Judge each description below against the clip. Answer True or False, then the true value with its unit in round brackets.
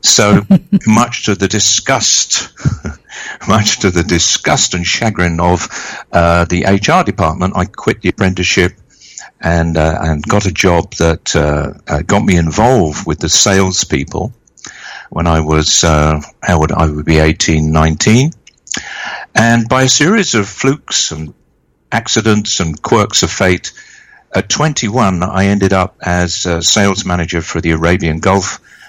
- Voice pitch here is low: True (90 Hz)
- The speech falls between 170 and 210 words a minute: False (145 wpm)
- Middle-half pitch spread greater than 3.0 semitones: True (4.5 semitones)